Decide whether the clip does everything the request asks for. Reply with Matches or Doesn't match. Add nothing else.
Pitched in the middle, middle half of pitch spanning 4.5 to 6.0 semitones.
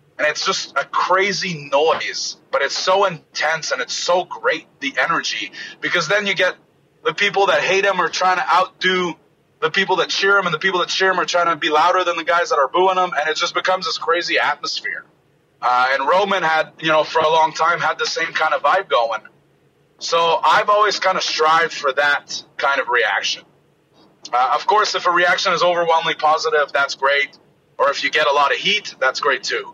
Doesn't match